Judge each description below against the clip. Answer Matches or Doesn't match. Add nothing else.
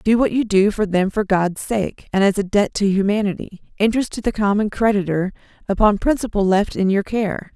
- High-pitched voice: Matches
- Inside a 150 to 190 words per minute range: Doesn't match